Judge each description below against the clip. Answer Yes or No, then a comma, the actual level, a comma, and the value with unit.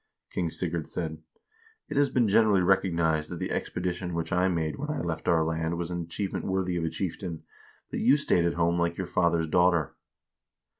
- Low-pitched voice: Yes, very low, 85 Hz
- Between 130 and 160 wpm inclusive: No, average, 200 wpm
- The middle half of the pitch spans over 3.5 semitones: No, narrow, 2.4 semitones